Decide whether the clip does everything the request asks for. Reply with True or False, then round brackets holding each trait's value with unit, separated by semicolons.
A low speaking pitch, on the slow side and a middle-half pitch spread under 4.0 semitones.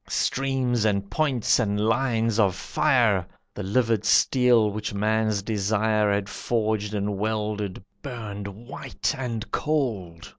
True (110 Hz; 120 wpm; 2.9 semitones)